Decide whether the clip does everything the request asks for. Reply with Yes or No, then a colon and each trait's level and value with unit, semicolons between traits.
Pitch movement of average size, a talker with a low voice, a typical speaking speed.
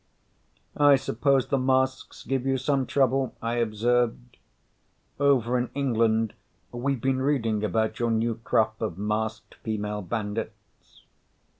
No: average, 3.2 semitones; low, 120 Hz; slow, 125 wpm